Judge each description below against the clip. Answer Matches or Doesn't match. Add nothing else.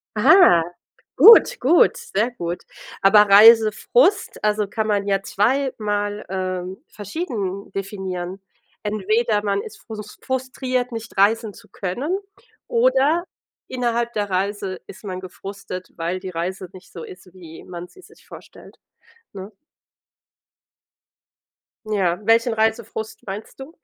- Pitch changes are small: Doesn't match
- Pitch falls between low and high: Doesn't match